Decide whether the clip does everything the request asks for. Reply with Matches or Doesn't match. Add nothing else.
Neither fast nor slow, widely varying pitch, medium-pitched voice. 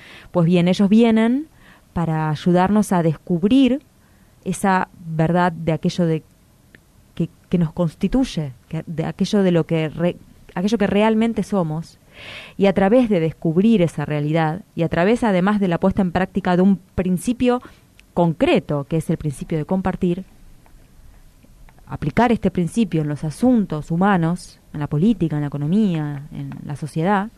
Doesn't match